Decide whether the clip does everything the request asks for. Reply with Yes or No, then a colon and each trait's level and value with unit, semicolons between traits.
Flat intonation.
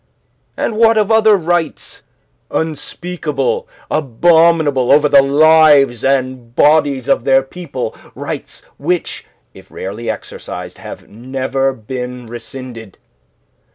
No: average, 4.3 semitones